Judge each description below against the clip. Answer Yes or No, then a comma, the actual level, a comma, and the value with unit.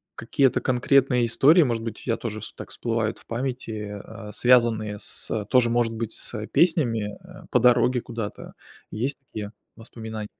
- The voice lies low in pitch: Yes, low, 115 Hz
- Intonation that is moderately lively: No, narrow, 2.2 semitones